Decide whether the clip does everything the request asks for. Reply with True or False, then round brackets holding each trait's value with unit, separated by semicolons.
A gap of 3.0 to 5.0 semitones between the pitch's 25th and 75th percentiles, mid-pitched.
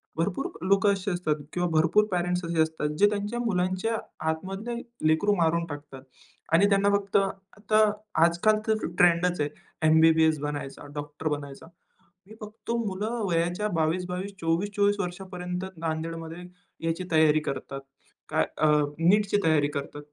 True (4.0 semitones; 175 Hz)